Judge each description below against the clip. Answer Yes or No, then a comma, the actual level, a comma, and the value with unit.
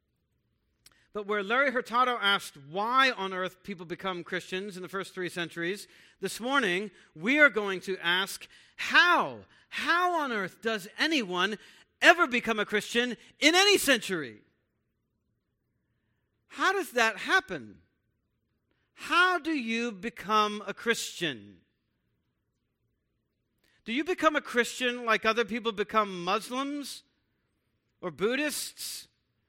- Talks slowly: Yes, slow, 120 wpm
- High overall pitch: Yes, high, 210 Hz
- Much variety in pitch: Yes, wide, 6.2 semitones